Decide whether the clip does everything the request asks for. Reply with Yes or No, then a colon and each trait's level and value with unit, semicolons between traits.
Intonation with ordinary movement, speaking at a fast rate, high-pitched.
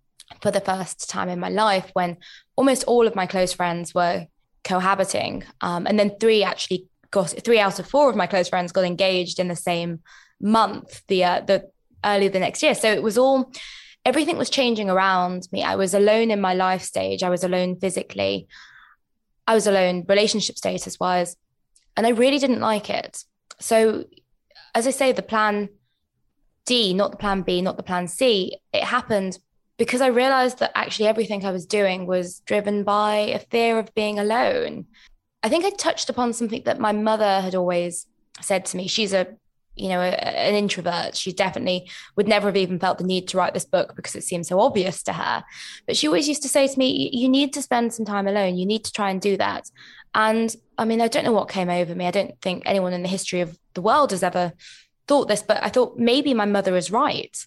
Yes: average, 3.9 semitones; fast, 215 wpm; high, 200 Hz